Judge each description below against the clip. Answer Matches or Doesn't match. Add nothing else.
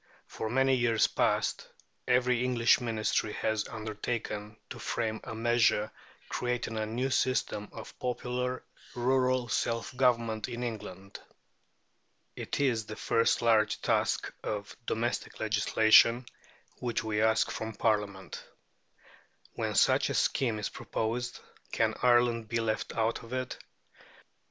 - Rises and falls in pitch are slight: Matches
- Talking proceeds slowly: Matches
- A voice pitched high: Doesn't match